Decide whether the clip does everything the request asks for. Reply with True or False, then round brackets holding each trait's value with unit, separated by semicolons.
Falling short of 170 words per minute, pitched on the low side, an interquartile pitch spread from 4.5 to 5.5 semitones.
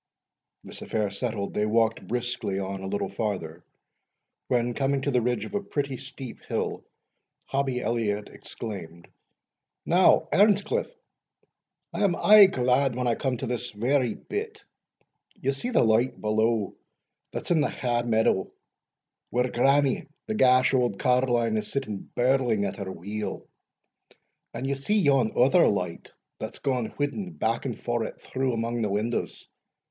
False (150 wpm; 125 Hz; 3.8 semitones)